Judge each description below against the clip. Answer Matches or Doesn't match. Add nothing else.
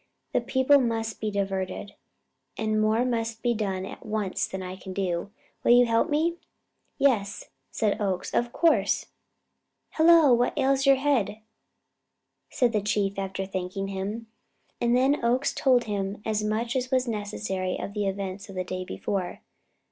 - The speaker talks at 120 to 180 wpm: Matches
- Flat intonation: Doesn't match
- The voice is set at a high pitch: Matches